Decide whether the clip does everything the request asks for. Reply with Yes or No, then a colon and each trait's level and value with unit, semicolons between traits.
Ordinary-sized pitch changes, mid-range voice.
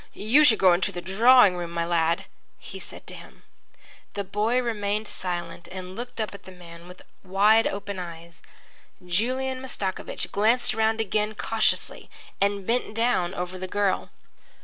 No: average, 3.7 semitones; high, 200 Hz